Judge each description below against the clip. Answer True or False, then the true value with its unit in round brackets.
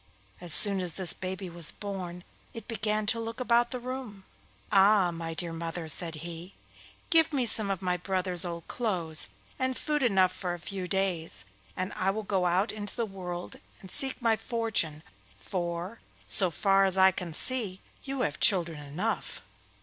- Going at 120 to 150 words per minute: False (175 wpm)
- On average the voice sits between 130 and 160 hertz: False (190 Hz)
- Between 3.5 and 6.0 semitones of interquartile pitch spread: True (3.9 semitones)